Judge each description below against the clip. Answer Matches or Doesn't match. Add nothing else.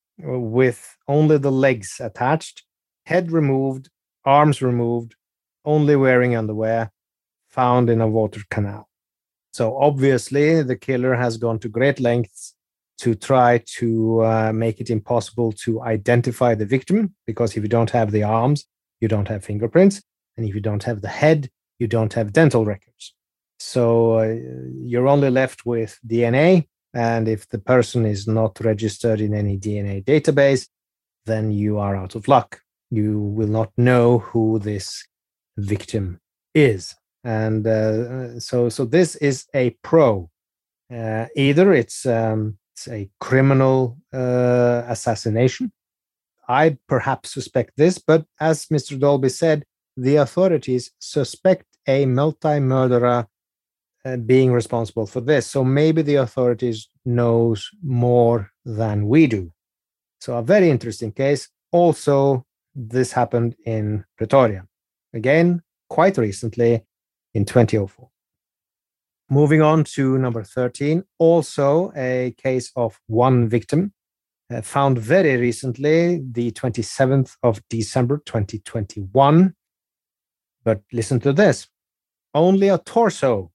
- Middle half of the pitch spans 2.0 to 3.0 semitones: Doesn't match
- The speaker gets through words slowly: Matches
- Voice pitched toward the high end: Doesn't match